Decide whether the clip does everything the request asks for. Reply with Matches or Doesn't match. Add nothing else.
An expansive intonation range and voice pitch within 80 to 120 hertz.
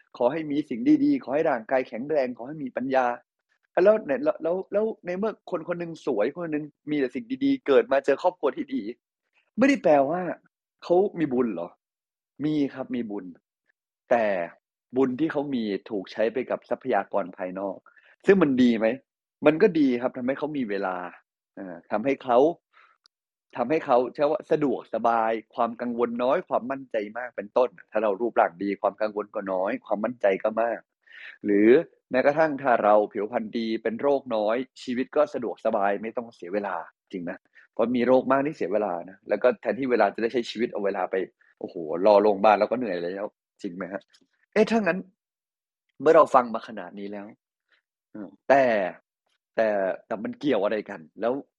Doesn't match